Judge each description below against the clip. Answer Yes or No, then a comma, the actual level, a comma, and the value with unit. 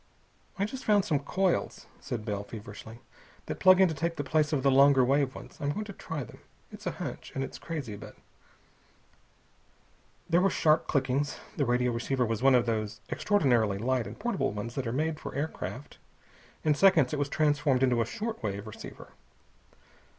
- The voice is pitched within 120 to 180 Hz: Yes, medium, 140 Hz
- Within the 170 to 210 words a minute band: Yes, average, 185 wpm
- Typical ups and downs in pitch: Yes, average, 4.9 semitones